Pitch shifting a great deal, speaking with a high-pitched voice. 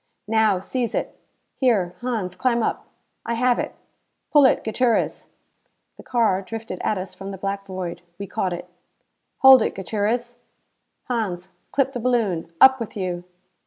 No: average, 4.5 semitones; high, 215 Hz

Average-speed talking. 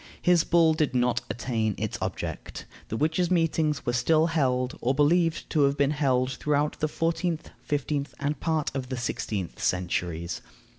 Yes: average, 160 wpm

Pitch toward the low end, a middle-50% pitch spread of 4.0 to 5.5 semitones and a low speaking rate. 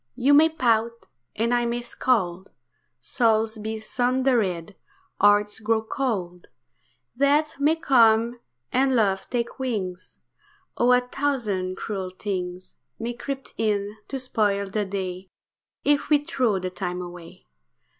No: high, 220 Hz; average, 4.7 semitones; slow, 125 wpm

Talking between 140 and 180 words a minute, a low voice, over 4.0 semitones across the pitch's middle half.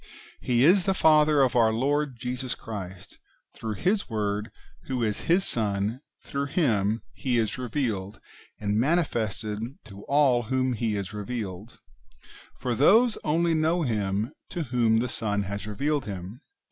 Yes: average, 150 wpm; low, 120 Hz; average, 5.3 semitones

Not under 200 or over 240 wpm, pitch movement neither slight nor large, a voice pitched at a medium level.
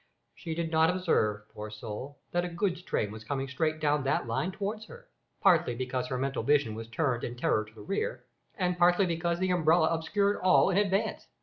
No: fast, 205 wpm; wide, 6.3 semitones; medium, 160 Hz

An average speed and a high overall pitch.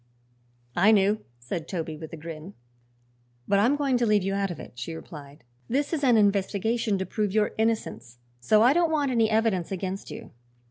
Yes: average, 190 wpm; high, 200 Hz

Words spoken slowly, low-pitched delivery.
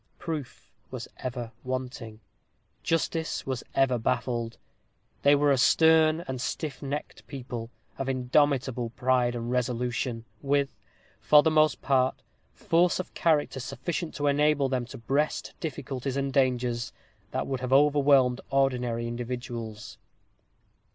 Yes: slow, 125 wpm; low, 130 Hz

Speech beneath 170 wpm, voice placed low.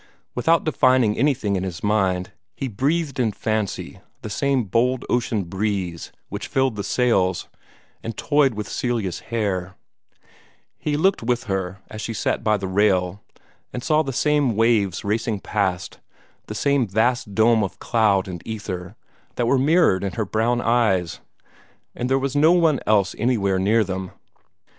Yes: average, 155 wpm; low, 110 Hz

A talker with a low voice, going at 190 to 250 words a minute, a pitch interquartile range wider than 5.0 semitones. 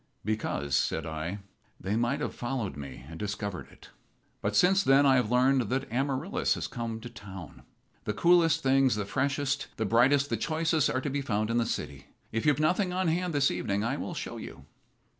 Yes: low, 125 Hz; average, 195 wpm; wide, 5.5 semitones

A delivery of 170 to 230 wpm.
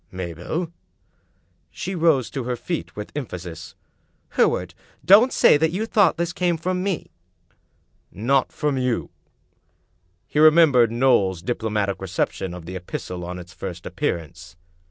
No: average, 140 wpm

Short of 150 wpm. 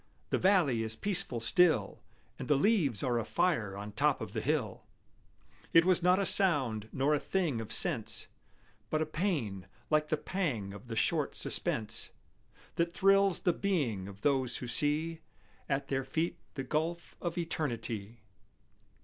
No: average, 160 wpm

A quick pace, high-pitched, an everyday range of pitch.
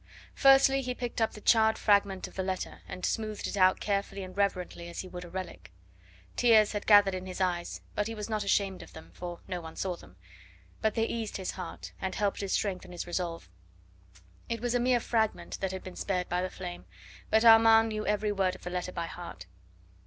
Yes: fast, 220 wpm; high, 195 Hz; average, 3.2 semitones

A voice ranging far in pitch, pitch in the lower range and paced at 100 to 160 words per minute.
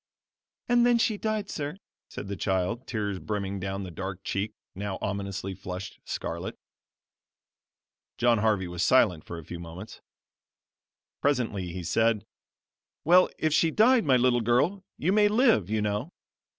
Yes: wide, 8.2 semitones; low, 105 Hz; average, 150 wpm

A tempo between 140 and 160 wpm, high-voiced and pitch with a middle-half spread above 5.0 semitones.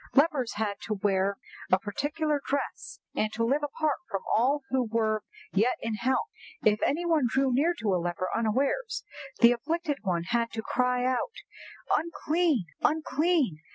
Yes: average, 155 wpm; very high, 250 Hz; wide, 5.5 semitones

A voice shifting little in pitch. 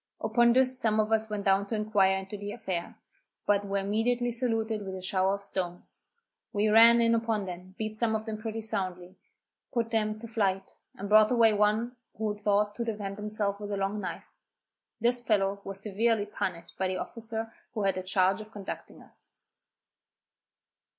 Yes: narrow, 2.3 semitones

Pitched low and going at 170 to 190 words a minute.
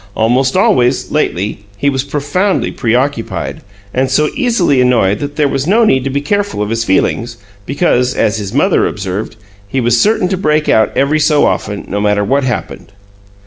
Yes: low, 130 Hz; average, 185 wpm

